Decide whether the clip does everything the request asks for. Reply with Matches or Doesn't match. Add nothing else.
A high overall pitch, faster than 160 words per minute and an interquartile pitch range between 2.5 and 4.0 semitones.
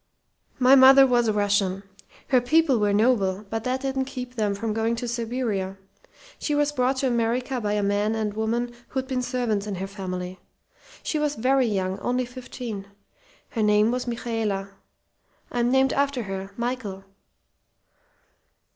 Doesn't match